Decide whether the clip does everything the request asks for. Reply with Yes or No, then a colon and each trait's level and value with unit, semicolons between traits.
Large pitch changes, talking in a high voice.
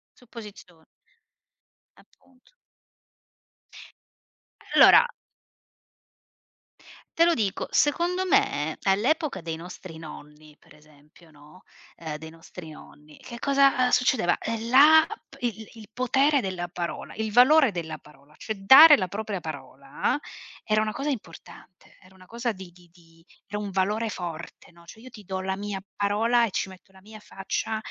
Yes: wide, 6.0 semitones; high, 200 Hz